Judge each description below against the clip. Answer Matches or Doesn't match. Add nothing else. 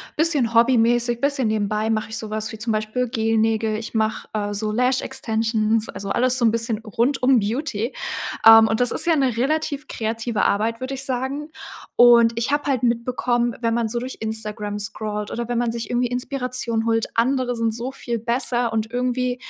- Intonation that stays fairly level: Matches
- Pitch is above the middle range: Matches